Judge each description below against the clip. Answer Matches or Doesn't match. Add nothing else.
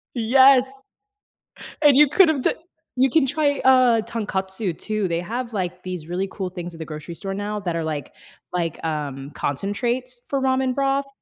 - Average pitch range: Doesn't match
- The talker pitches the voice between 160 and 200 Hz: Doesn't match